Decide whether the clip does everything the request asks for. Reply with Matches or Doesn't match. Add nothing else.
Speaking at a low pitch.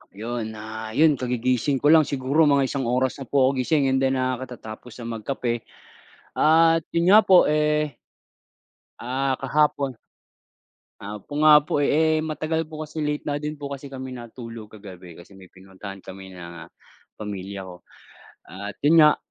Matches